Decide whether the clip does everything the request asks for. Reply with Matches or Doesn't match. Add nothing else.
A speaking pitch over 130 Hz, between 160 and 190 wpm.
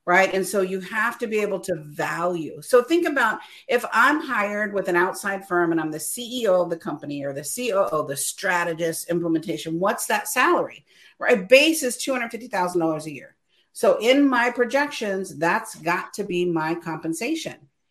Matches